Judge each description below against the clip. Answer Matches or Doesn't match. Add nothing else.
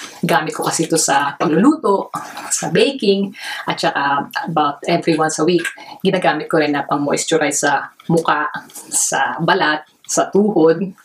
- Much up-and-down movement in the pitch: Doesn't match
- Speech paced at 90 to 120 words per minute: Doesn't match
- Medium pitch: Matches